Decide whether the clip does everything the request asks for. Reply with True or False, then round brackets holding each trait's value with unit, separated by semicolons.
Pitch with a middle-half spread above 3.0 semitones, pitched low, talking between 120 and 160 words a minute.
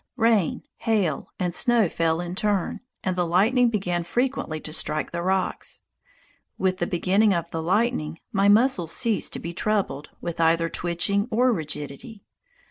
False (4.5 semitones; 185 Hz; 155 wpm)